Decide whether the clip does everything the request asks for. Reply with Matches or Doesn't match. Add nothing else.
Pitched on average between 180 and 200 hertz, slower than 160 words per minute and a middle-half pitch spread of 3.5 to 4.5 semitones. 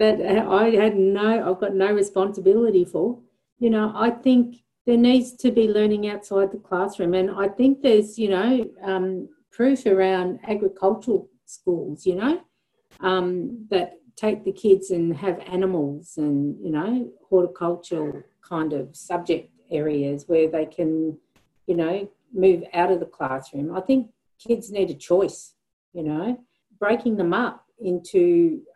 Matches